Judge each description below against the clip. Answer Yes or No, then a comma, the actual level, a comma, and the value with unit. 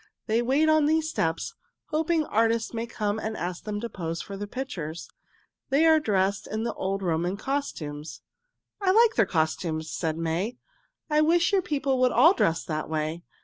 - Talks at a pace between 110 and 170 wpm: No, average, 180 wpm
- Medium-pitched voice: No, high, 220 Hz